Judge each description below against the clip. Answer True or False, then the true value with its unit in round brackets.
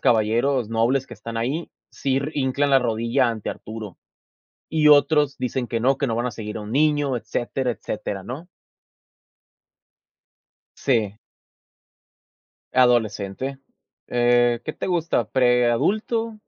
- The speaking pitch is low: True (125 Hz)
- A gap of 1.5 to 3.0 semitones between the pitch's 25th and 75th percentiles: False (3.4 semitones)